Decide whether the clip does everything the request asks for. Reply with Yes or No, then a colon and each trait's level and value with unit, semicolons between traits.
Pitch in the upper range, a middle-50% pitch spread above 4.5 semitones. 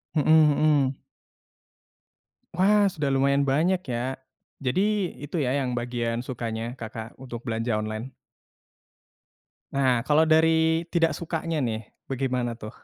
No: low, 135 Hz; average, 5.1 semitones